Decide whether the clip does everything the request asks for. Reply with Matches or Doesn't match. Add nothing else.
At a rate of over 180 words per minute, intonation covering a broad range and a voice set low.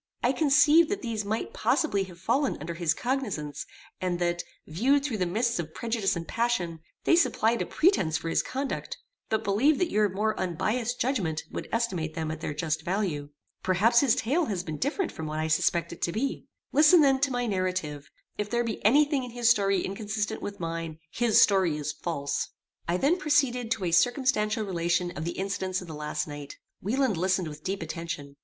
Doesn't match